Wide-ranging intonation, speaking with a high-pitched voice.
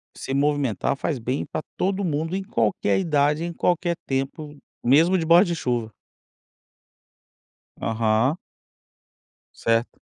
No: wide, 5.7 semitones; medium, 145 Hz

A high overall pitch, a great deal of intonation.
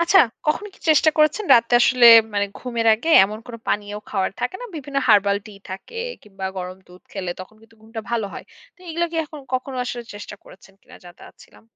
Yes: high, 230 Hz; wide, 6.1 semitones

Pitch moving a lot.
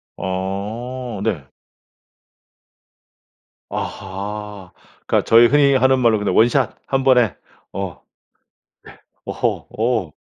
No: average, 4.5 semitones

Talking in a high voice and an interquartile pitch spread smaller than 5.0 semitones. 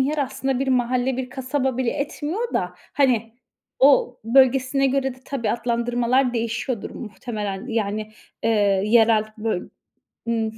Yes: high, 245 Hz; average, 2.9 semitones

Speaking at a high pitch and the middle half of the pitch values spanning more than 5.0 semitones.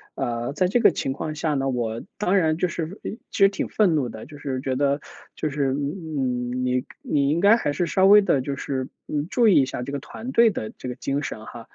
No: medium, 145 Hz; wide, 5.5 semitones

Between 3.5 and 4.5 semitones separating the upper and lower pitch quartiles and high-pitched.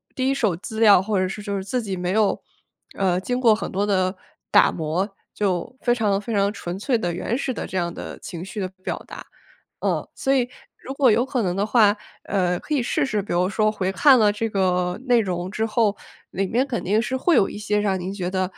Yes: average, 3.8 semitones; high, 205 Hz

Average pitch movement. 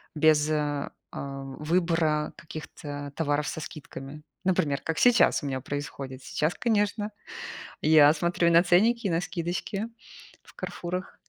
Yes: average, 3.4 semitones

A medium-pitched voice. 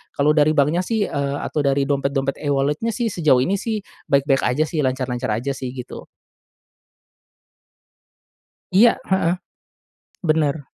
Yes: medium, 145 Hz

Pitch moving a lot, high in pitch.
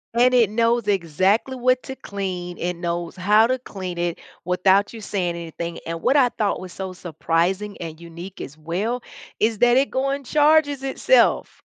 Yes: wide, 5.9 semitones; high, 195 Hz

